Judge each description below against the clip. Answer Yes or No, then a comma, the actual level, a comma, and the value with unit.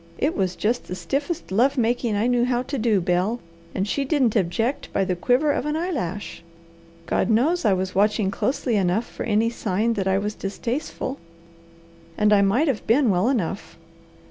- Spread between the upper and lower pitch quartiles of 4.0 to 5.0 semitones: Yes, average, 4.7 semitones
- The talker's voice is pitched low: No, high, 225 Hz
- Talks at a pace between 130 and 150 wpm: No, average, 185 wpm